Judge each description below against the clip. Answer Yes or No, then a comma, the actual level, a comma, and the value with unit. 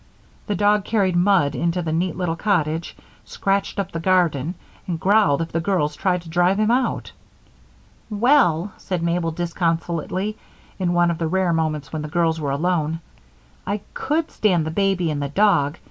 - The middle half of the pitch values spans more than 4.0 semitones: No, average, 3.3 semitones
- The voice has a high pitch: No, medium, 175 Hz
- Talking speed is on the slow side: No, average, 175 wpm